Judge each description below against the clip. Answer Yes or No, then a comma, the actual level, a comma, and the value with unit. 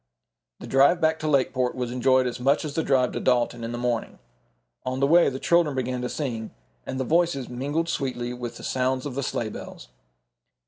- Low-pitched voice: Yes, low, 130 Hz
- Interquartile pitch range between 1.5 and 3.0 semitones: Yes, narrow, 2.5 semitones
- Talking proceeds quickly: Yes, fast, 210 wpm